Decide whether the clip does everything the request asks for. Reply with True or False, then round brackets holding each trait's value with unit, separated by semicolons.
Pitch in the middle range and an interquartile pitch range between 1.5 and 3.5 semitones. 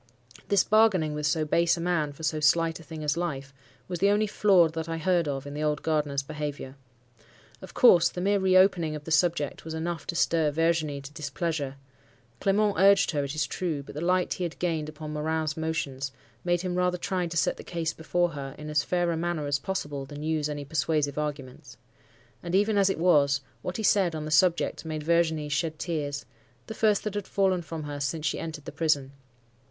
True (160 Hz; 3.0 semitones)